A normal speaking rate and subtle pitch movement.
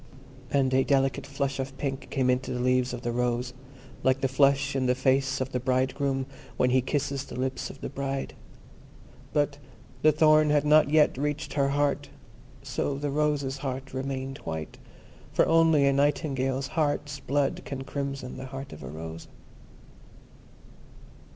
Yes: average, 165 wpm; narrow, 1.6 semitones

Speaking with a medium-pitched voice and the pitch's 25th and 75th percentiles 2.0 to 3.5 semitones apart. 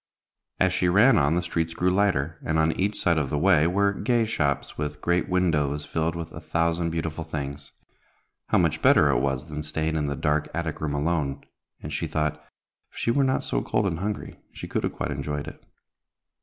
No: very low, 80 Hz; average, 3.2 semitones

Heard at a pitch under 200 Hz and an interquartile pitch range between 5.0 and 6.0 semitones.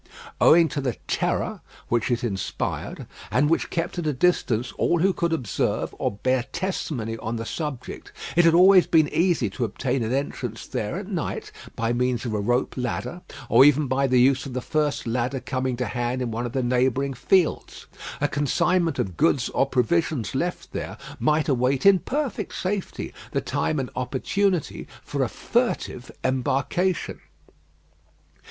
Yes: low, 135 Hz; average, 5.3 semitones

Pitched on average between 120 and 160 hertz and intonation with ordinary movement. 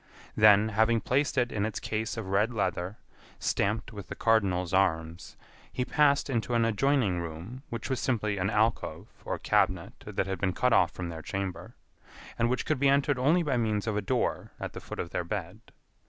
No: low, 110 Hz; average, 4.3 semitones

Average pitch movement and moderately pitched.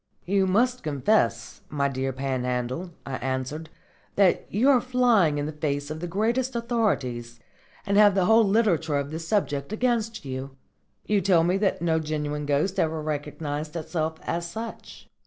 No: wide, 6.4 semitones; medium, 160 Hz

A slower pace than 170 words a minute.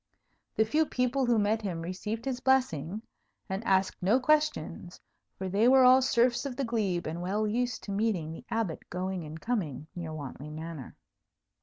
No: average, 175 wpm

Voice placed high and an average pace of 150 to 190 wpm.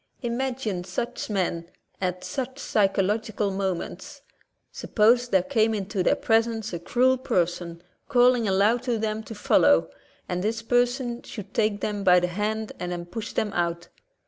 Yes: high, 210 Hz; average, 155 wpm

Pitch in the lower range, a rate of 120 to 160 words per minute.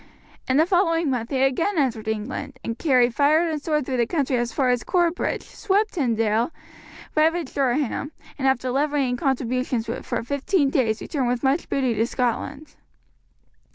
No: very high, 270 Hz; average, 155 wpm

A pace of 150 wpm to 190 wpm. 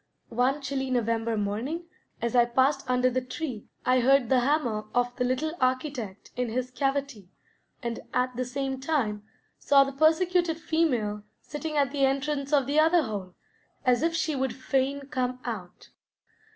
Yes: average, 165 wpm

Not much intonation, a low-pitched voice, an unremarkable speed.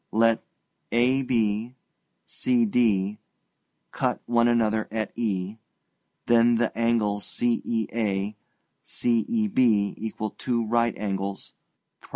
No: narrow, 2.1 semitones; low, 115 Hz; slow, 90 wpm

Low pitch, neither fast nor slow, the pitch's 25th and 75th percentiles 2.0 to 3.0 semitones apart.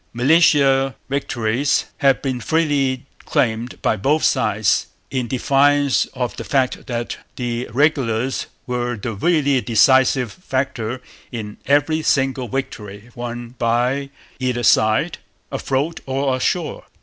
No: low, 130 Hz; slow, 115 wpm; average, 2.7 semitones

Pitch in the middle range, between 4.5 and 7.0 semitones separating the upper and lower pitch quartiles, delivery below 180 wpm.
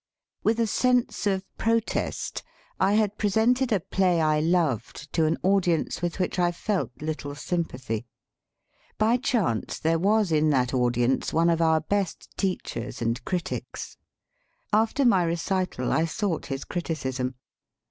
Yes: medium, 175 Hz; average, 5.2 semitones; average, 145 wpm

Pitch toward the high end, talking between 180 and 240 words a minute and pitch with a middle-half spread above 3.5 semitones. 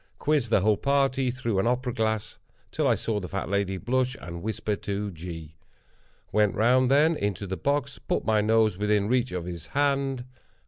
No: low, 110 Hz; average, 190 wpm; average, 4.7 semitones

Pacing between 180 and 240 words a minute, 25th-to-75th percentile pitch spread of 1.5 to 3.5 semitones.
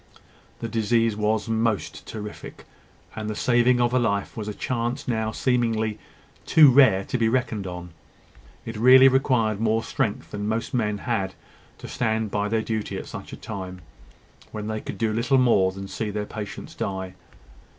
No: average, 170 wpm; narrow, 2.4 semitones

